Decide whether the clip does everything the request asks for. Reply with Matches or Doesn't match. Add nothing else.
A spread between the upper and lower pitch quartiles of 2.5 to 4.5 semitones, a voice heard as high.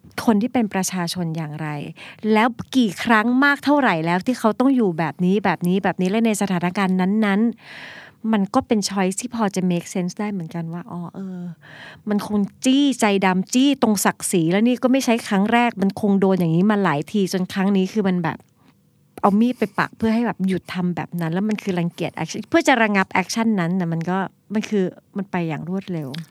Matches